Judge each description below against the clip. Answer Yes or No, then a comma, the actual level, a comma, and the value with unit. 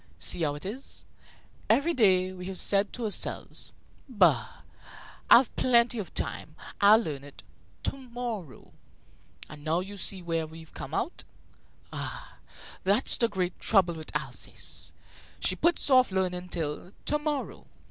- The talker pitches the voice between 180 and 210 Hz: Yes, high, 190 Hz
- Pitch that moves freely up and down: Yes, wide, 6.2 semitones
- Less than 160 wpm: Yes, average, 145 wpm